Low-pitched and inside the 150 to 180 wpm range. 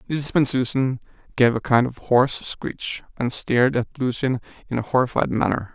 Yes: low, 125 Hz; average, 165 wpm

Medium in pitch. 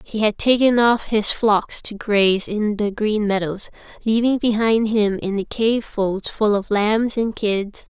No: high, 215 Hz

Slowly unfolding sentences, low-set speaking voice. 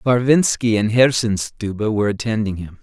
Yes: slow, 125 wpm; low, 110 Hz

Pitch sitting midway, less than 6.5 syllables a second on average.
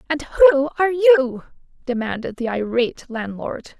No: very high, 270 Hz; 4.6 syllables/s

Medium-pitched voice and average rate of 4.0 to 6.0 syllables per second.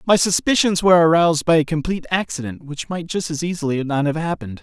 No: medium, 160 Hz; 6.4 syllables/s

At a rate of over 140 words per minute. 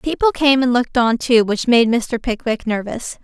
Yes: fast, 205 wpm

